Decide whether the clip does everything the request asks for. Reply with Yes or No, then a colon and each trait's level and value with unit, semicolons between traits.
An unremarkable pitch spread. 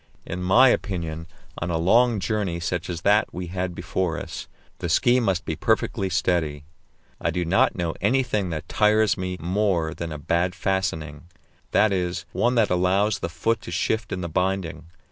Yes: average, 3.4 semitones